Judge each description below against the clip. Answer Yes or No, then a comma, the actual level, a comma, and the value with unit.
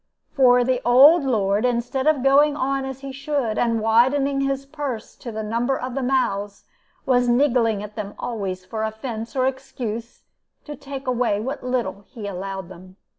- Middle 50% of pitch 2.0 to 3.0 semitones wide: No, average, 3.7 semitones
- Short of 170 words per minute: No, average, 175 wpm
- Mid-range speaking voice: No, high, 245 Hz